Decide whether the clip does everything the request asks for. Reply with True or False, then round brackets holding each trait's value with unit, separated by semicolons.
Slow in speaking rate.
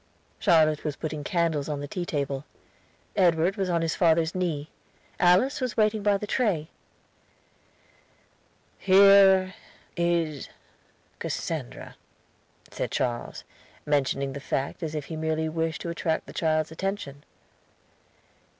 True (125 wpm)